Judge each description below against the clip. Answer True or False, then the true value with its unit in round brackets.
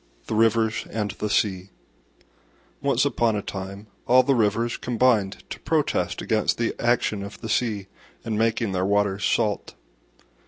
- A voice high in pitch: False (110 Hz)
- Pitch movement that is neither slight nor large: False (2.3 semitones)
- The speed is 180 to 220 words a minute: False (150 wpm)